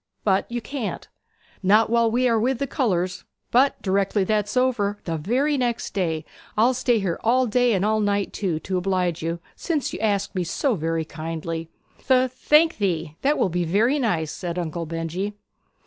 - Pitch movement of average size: No, wide, 5.8 semitones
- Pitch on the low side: No, high, 205 Hz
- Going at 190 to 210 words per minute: No, average, 180 wpm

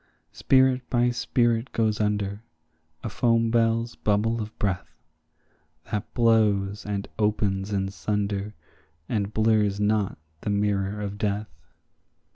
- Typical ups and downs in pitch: No, narrow, 2.1 semitones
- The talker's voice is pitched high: No, low, 105 Hz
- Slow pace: Yes, slow, 115 wpm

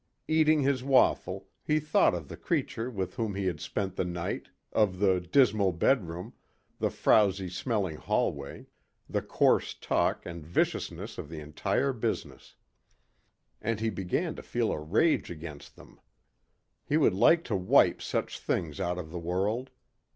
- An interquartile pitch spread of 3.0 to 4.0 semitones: No, average, 5.1 semitones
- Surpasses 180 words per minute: No, average, 155 wpm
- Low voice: Yes, very low, 95 Hz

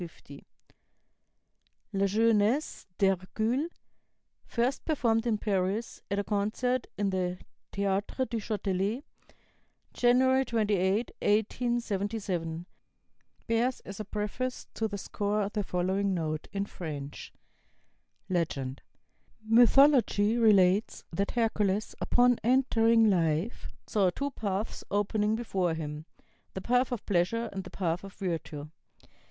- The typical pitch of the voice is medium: No, high, 205 Hz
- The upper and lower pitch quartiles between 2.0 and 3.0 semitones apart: No, average, 3.6 semitones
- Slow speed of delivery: Yes, slow, 110 wpm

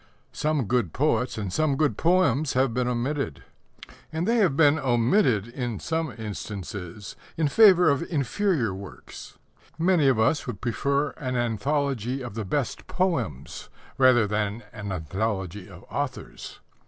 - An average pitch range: No, wide, 5.9 semitones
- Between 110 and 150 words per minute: Yes, average, 140 wpm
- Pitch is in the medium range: No, low, 125 Hz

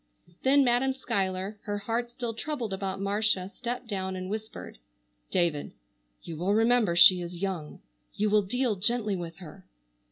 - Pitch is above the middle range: Yes, high, 205 Hz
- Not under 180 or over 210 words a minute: No, average, 155 wpm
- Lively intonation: No, average, 4.1 semitones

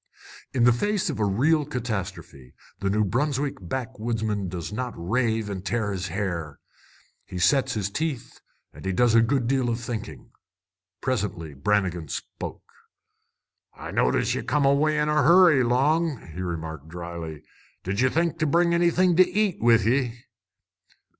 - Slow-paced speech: No, average, 155 wpm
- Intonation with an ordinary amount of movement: No, wide, 7.0 semitones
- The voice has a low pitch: Yes, low, 115 Hz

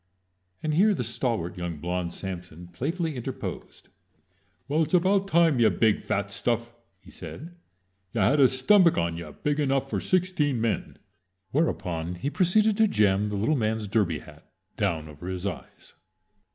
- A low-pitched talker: Yes, low, 115 Hz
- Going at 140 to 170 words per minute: Yes, average, 165 wpm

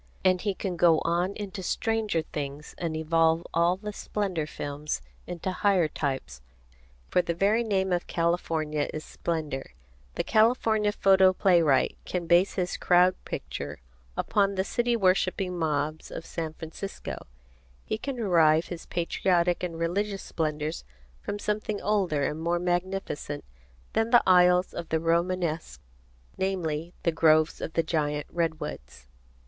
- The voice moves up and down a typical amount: Yes, average, 3.4 semitones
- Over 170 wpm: No, average, 140 wpm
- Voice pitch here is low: No, medium, 175 Hz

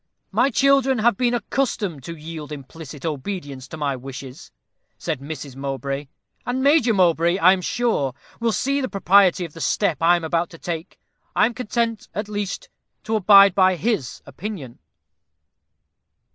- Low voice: No, medium, 180 Hz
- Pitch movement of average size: No, wide, 6.7 semitones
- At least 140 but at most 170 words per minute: Yes, average, 160 wpm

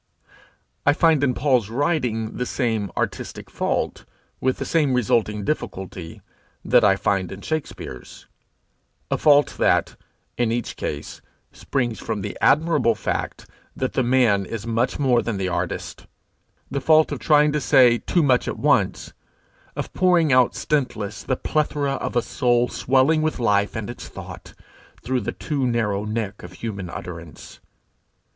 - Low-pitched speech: Yes, low, 120 Hz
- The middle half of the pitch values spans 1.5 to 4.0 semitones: No, average, 5.3 semitones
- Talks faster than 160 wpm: No, average, 150 wpm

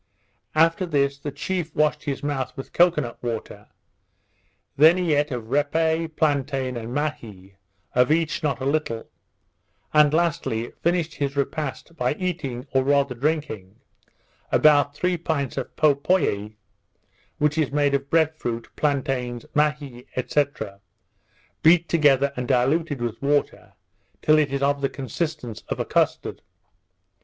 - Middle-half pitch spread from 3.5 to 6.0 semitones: No, average, 3.1 semitones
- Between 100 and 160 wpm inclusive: Yes, average, 140 wpm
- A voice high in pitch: No, medium, 145 Hz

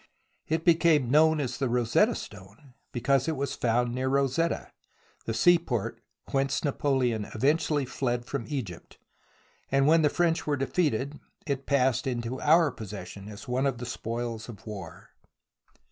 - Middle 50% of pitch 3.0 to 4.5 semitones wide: Yes, average, 3.8 semitones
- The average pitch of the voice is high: No, low, 130 Hz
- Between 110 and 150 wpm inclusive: Yes, average, 145 wpm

